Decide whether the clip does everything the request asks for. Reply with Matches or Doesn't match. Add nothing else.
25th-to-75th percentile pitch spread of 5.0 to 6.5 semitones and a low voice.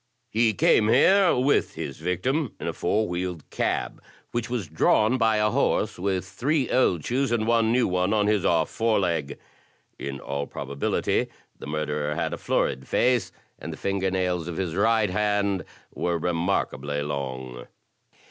Matches